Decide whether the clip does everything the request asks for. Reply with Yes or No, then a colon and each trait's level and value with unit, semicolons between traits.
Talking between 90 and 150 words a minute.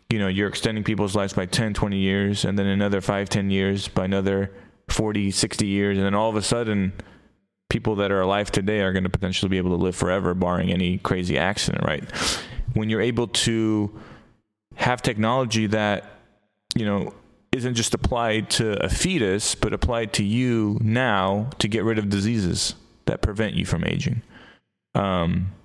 No: average, 180 wpm